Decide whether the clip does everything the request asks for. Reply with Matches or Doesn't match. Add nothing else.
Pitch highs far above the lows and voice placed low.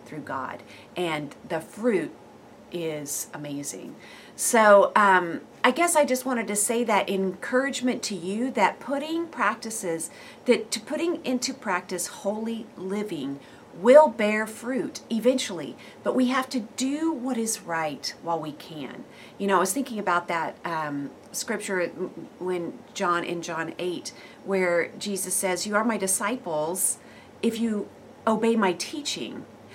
Doesn't match